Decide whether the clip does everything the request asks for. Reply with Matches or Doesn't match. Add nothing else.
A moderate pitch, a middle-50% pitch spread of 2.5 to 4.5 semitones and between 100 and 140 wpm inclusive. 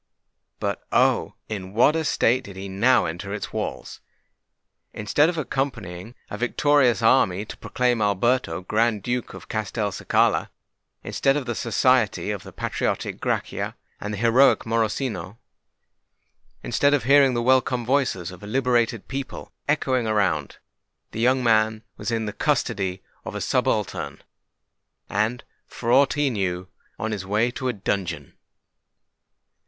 Doesn't match